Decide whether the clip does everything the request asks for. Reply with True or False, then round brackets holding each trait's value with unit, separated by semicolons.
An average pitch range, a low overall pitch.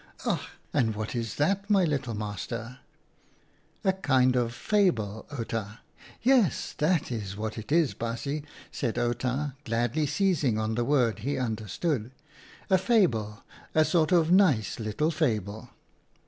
False (6.3 semitones; 125 Hz)